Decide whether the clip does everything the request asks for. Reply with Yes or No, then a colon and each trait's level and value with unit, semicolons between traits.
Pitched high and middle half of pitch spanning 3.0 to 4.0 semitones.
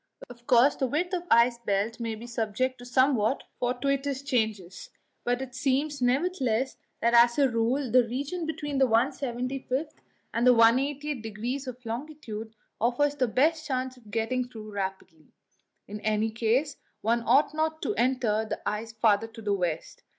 Yes: high, 245 Hz; average, 3.5 semitones